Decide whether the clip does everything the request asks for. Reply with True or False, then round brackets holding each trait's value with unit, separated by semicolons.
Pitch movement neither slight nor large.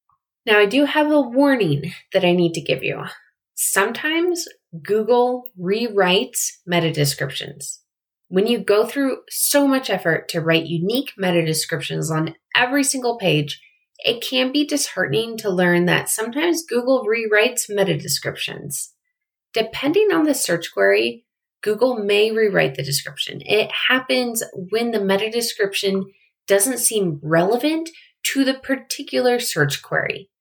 False (7.4 semitones)